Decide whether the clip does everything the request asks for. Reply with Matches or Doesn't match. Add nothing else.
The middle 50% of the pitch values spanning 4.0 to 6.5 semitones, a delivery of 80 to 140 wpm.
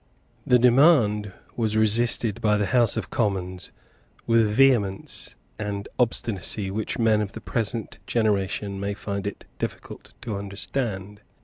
Doesn't match